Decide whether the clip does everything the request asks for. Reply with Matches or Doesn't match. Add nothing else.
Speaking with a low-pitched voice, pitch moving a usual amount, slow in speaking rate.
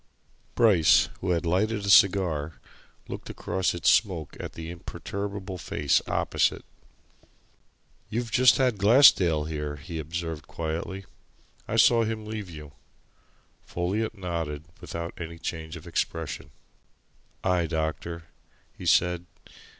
Matches